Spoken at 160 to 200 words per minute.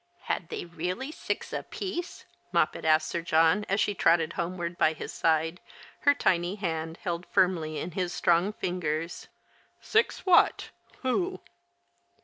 No: average, 145 wpm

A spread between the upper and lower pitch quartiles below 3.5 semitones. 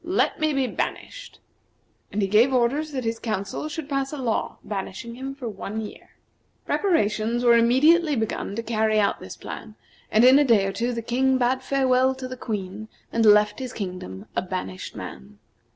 No: average, 3.9 semitones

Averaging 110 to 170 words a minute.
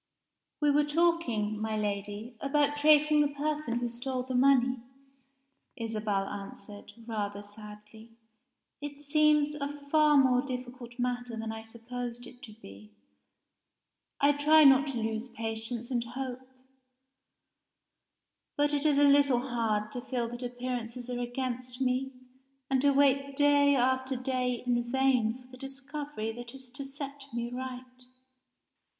Yes: average, 140 wpm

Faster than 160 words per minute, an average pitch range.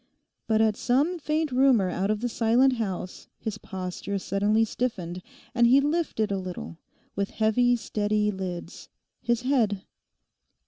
No: average, 140 wpm; average, 4.0 semitones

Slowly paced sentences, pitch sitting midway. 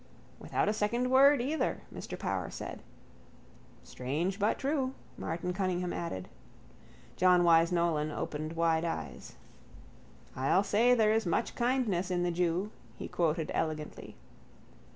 Yes: slow, 130 wpm; medium, 180 Hz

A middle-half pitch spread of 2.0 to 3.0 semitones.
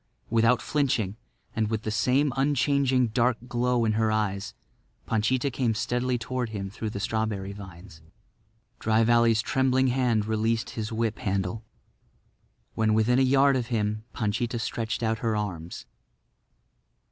Yes: narrow, 2.5 semitones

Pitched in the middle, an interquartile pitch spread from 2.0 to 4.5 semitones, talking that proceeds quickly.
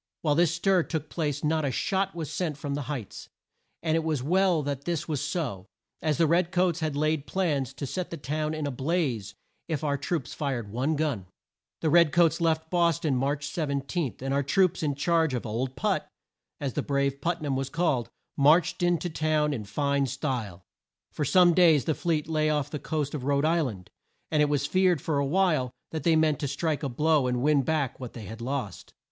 Yes: medium, 150 Hz; average, 3.2 semitones; fast, 215 wpm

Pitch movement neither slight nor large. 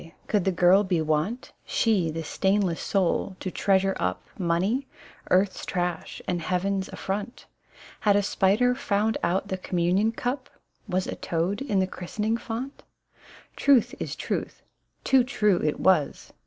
Yes: average, 3.3 semitones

